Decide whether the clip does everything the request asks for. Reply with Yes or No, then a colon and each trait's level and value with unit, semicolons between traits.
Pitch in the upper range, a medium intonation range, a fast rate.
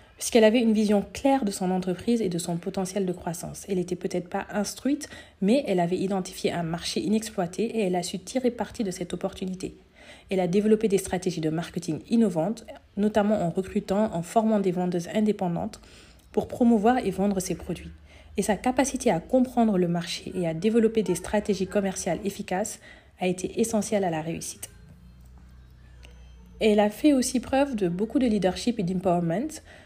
No: high, 195 Hz; average, 3.6 semitones; average, 175 wpm